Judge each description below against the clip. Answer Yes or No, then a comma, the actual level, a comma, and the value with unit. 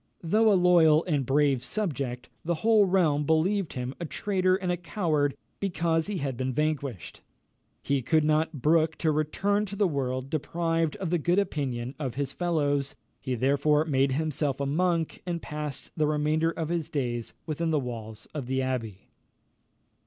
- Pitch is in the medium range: Yes, medium, 155 Hz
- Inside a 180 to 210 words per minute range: No, average, 170 wpm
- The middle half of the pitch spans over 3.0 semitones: Yes, average, 3.9 semitones